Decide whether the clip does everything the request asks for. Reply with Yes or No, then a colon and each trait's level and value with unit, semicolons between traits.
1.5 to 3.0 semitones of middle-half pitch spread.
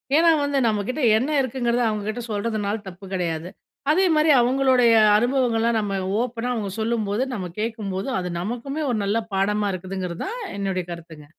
No: average, 4.2 semitones